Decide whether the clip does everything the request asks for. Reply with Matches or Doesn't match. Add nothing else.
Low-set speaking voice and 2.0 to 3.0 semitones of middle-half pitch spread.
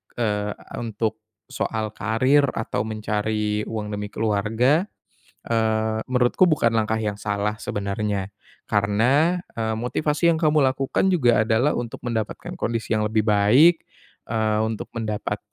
Matches